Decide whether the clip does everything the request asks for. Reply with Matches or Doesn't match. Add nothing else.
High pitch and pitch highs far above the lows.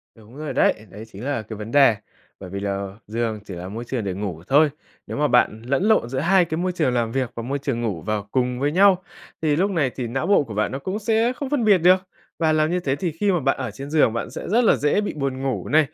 Doesn't match